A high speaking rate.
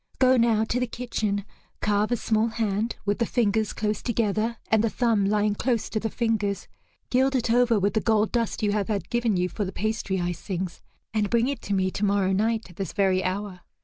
Yes: fast, 215 wpm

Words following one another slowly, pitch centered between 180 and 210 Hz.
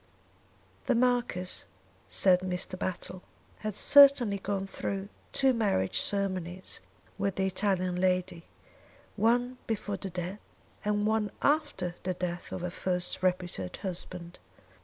Yes: slow, 120 wpm; high, 190 Hz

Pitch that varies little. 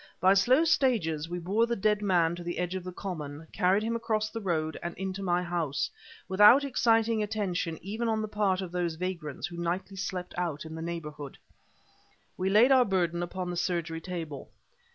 No: average, 3.7 semitones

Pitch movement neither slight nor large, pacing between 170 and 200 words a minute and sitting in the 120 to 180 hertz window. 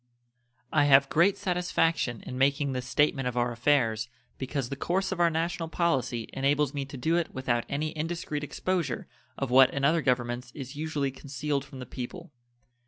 Yes: average, 3.9 semitones; average, 175 wpm; medium, 140 Hz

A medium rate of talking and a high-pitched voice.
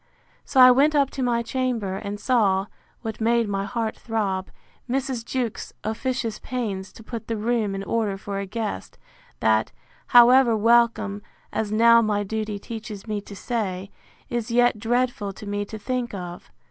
Yes: average, 165 wpm; high, 220 Hz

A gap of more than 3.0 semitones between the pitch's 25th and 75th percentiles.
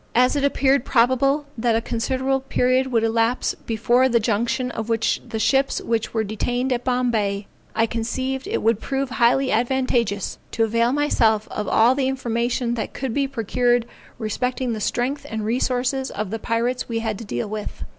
No: narrow, 2.5 semitones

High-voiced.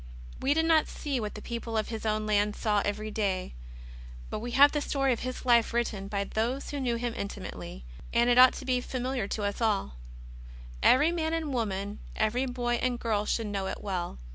Yes: high, 235 Hz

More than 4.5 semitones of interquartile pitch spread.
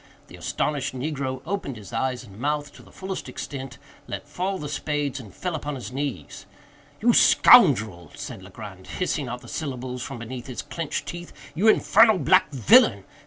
Yes: average, 5.1 semitones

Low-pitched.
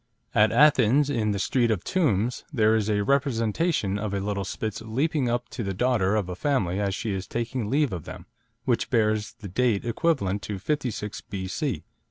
Yes: low, 110 Hz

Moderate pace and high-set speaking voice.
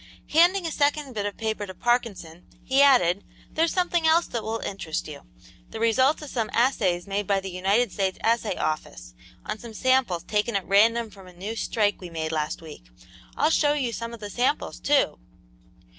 Yes: average, 190 wpm; high, 220 Hz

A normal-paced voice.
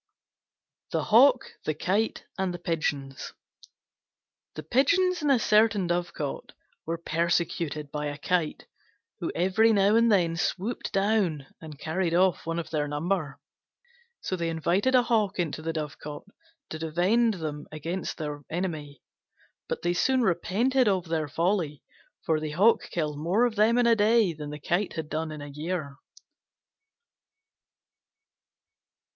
Yes: average, 145 wpm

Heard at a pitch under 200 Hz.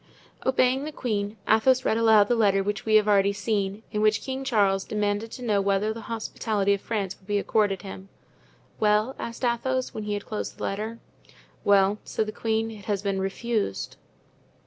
No: high, 210 Hz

